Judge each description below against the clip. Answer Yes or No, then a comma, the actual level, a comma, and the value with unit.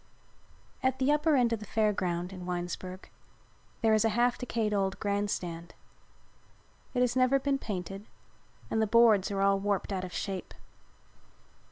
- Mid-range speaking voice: No, high, 205 Hz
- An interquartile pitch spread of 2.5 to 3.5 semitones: No, average, 4.1 semitones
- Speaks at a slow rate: No, average, 165 wpm